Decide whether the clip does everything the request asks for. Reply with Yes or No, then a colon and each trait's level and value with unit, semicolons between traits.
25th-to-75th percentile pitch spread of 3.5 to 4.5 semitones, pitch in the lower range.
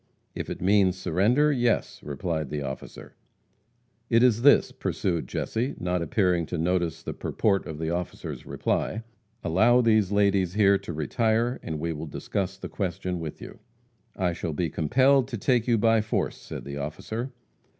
No: wide, 5.4 semitones; very low, 95 Hz